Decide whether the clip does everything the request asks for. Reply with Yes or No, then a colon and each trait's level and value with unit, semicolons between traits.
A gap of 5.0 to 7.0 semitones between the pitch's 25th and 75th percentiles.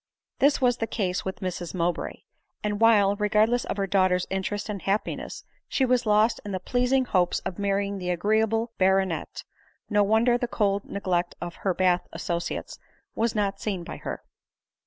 No: average, 3.0 semitones